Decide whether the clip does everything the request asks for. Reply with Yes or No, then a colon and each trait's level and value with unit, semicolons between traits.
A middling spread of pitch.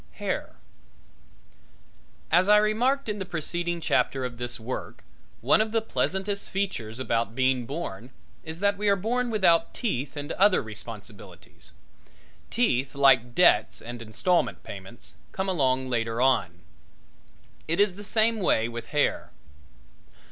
No: wide, 8.9 semitones